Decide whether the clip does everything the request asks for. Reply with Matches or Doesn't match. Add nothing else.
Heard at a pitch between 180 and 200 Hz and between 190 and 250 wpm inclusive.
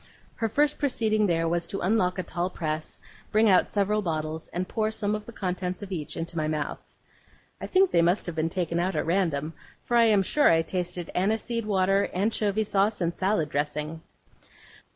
Matches